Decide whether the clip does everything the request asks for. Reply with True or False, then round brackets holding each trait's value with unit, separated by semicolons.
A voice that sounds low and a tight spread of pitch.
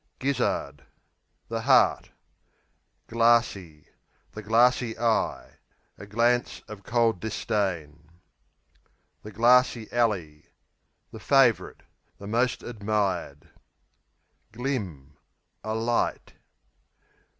False (110 Hz; 3.8 semitones)